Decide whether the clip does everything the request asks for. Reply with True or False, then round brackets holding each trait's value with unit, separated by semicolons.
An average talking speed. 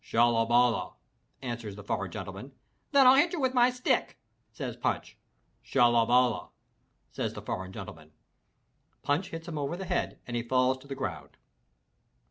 True (150 wpm)